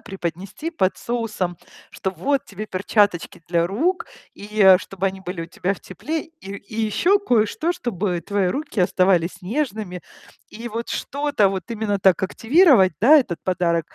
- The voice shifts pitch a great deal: No, average, 4.7 semitones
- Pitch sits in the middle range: No, high, 200 Hz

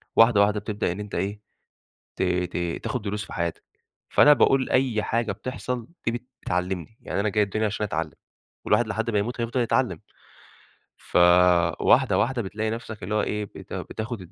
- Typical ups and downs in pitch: Yes, average, 3.8 semitones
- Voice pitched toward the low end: Yes, low, 105 Hz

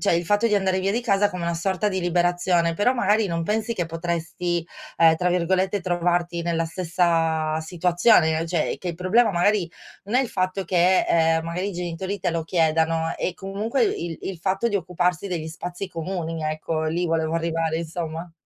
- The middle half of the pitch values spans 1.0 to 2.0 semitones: No, narrow, 2.5 semitones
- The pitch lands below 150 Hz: No, medium, 175 Hz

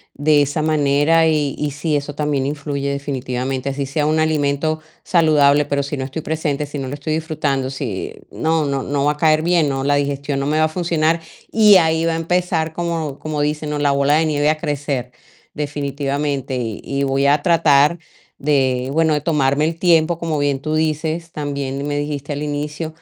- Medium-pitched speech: Yes, medium, 145 Hz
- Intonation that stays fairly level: Yes, narrow, 2.0 semitones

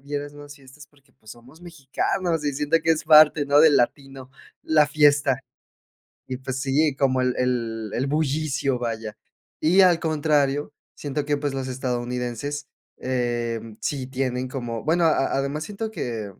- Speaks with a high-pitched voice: No, medium, 140 Hz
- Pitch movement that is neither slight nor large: Yes, average, 3.0 semitones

